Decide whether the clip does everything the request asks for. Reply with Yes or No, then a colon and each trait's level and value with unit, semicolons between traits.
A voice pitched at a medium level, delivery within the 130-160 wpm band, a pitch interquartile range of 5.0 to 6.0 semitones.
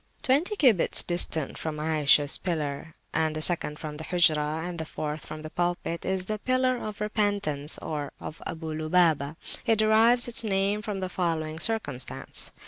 No: medium, 170 Hz; average, 170 wpm; average, 5.3 semitones